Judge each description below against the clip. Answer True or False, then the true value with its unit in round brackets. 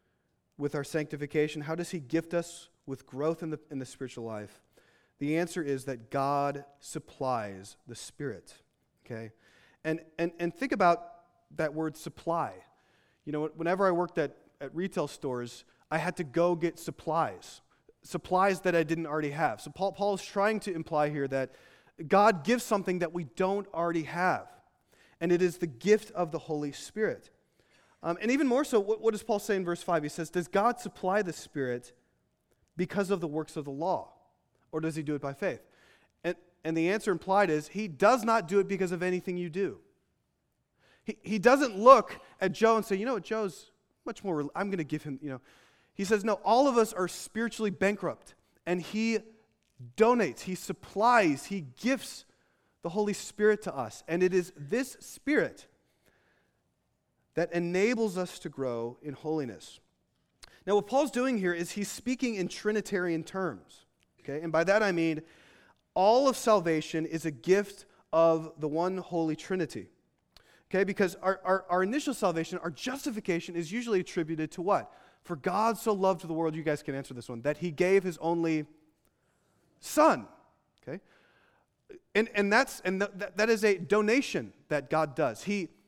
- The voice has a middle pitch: True (175 Hz)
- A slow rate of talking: False (180 wpm)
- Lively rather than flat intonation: False (4.6 semitones)